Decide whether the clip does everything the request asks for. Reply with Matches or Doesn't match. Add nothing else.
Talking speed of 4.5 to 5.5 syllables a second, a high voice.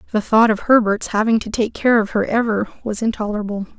Doesn't match